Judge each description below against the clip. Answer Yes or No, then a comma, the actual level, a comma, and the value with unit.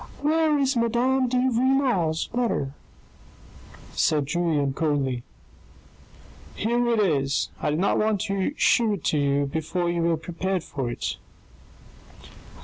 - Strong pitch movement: Yes, wide, 8.3 semitones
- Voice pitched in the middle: Yes, medium, 180 Hz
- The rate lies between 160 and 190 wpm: No, average, 140 wpm